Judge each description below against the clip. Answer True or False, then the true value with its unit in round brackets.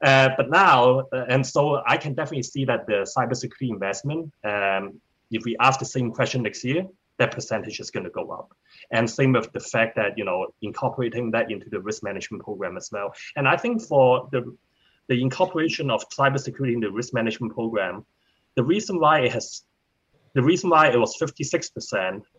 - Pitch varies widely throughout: False (4.2 semitones)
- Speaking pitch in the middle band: False (130 Hz)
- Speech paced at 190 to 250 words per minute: True (200 wpm)